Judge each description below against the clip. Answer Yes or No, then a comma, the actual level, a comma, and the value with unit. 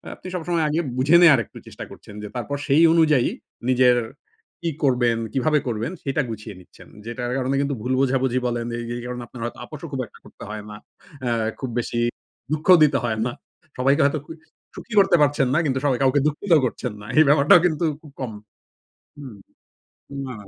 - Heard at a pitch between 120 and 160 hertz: Yes, low, 135 Hz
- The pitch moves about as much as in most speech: Yes, average, 3.7 semitones